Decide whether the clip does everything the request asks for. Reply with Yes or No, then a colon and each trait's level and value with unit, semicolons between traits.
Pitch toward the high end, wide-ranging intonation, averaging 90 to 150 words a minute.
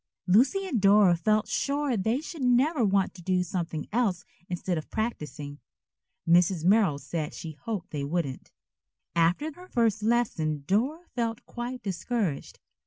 Yes: high, 200 Hz; wide, 6.1 semitones; average, 145 wpm